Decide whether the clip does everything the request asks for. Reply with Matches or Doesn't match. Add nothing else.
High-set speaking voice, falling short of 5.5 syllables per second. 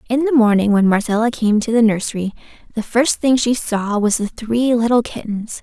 Matches